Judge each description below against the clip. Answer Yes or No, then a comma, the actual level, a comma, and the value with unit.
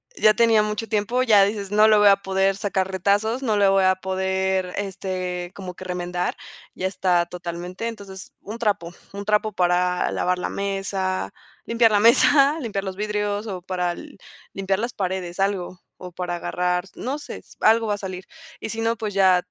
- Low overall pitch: No, high, 195 Hz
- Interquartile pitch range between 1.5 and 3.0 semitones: Yes, narrow, 2.5 semitones